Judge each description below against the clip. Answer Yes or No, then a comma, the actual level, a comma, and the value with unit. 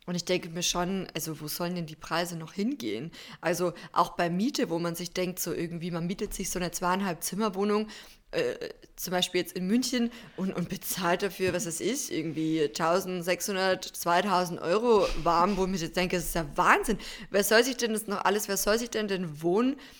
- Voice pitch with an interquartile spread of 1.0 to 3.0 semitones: No, average, 3.4 semitones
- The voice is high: No, medium, 180 Hz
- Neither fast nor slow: No, fast, 210 wpm